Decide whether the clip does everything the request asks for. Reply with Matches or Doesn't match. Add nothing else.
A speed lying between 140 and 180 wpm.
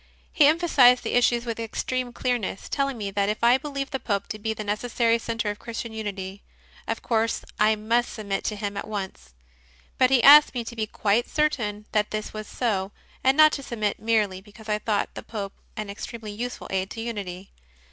Doesn't match